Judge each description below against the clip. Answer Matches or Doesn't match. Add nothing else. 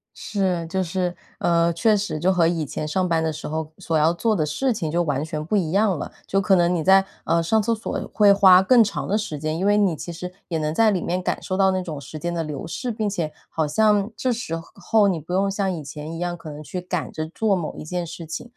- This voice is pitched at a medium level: Matches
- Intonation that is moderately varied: Matches